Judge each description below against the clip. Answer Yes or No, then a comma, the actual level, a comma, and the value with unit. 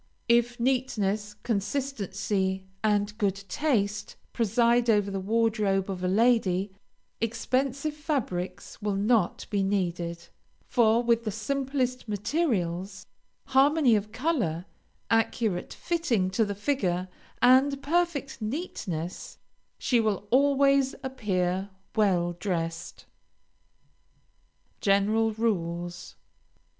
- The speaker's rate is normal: No, slow, 95 wpm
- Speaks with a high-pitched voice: Yes, high, 215 Hz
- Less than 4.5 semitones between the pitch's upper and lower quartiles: No, average, 4.8 semitones